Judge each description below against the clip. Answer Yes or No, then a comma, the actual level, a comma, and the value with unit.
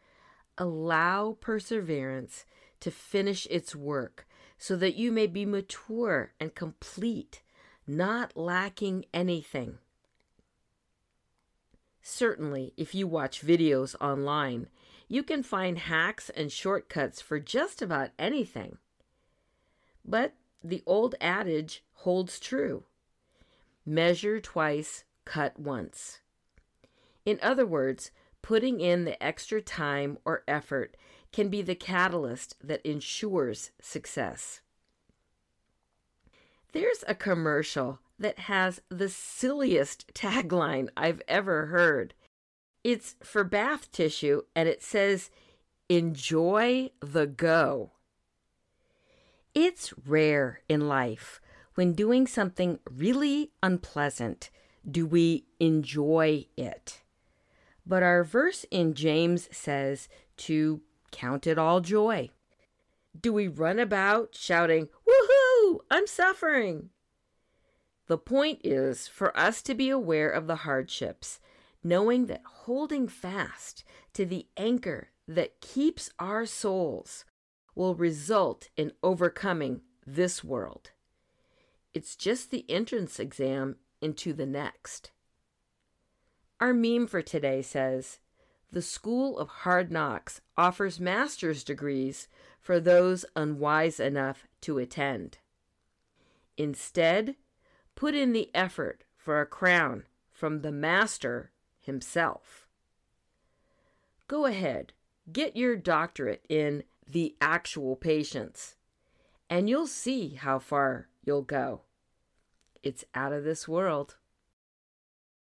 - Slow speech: Yes, slow, 105 wpm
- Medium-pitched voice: Yes, medium, 175 Hz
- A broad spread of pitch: Yes, wide, 6.3 semitones